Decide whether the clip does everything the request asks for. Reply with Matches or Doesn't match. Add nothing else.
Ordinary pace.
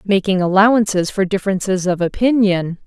Doesn't match